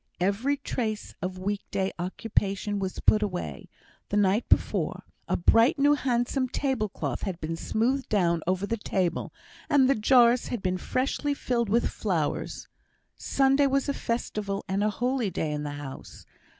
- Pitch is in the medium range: No, high, 210 Hz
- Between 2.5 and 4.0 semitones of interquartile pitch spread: No, average, 5.2 semitones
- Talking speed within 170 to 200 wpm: No, average, 160 wpm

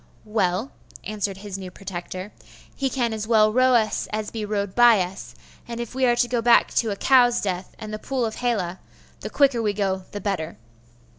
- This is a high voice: Yes, high, 215 Hz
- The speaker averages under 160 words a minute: No, fast, 205 wpm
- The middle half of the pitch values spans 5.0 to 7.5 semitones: No, average, 3.5 semitones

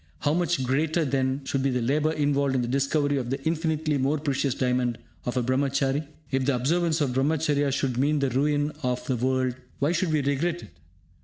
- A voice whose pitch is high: No, medium, 140 Hz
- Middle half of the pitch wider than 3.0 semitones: No, narrow, 2.6 semitones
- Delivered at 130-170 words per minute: No, fast, 205 wpm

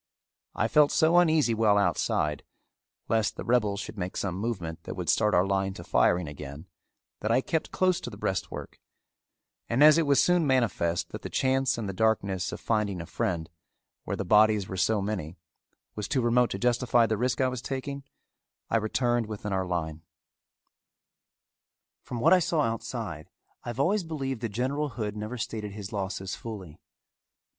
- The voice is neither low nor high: No, low, 110 Hz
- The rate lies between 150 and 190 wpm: Yes, average, 180 wpm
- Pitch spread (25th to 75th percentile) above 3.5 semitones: Yes, average, 4.9 semitones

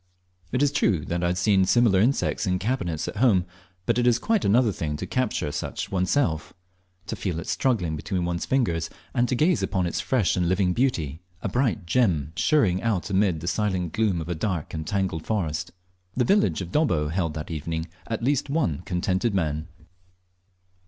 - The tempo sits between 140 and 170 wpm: No, average, 185 wpm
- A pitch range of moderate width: No, wide, 6.1 semitones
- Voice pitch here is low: Yes, very low, 95 Hz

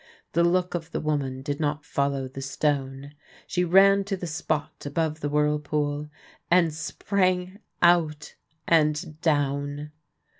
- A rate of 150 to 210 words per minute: No, slow, 135 wpm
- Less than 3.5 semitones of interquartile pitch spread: Yes, average, 3.0 semitones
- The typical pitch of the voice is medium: Yes, medium, 150 Hz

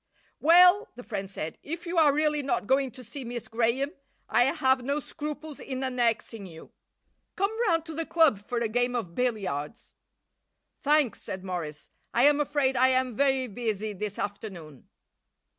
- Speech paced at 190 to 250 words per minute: No, average, 165 wpm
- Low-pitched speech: No, very high, 250 Hz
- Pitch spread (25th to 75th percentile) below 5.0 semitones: No, wide, 5.6 semitones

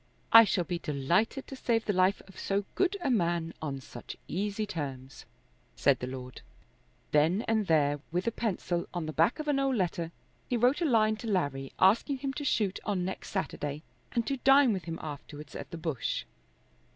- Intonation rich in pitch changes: Yes, wide, 6.7 semitones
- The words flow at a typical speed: Yes, average, 195 wpm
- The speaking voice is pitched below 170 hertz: No, medium, 185 Hz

